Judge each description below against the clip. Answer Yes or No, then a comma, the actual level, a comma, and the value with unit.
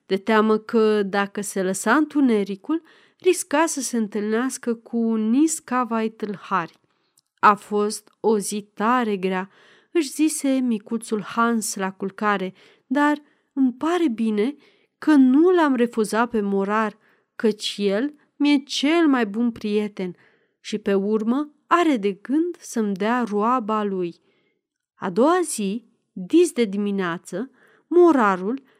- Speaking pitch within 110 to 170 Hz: No, high, 230 Hz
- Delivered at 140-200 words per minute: No, average, 125 wpm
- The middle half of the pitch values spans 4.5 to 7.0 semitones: Yes, wide, 5.6 semitones